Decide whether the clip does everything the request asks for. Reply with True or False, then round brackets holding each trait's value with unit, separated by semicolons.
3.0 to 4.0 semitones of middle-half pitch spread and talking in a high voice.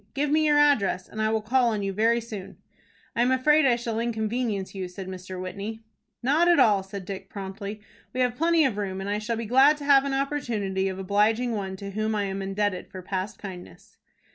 False (4.5 semitones; 215 Hz)